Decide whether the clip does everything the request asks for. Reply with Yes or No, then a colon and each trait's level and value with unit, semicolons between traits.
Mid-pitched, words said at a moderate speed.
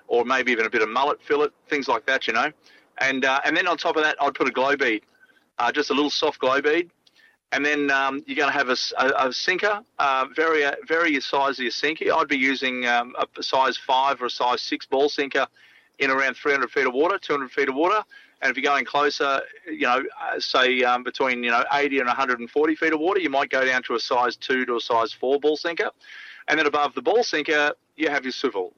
No: medium, 145 Hz; fast, 250 wpm